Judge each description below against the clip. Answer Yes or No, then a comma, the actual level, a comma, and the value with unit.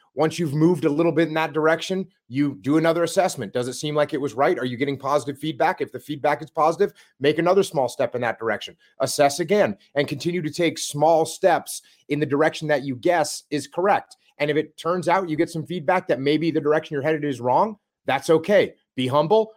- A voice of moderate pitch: Yes, medium, 155 Hz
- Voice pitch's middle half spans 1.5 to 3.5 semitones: Yes, narrow, 2.6 semitones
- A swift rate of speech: Yes, fast, 225 wpm